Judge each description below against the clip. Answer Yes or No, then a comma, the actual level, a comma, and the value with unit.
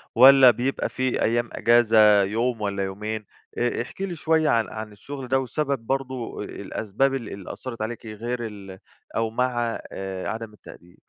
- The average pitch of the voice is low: Yes, low, 115 Hz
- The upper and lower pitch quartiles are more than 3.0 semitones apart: Yes, average, 3.4 semitones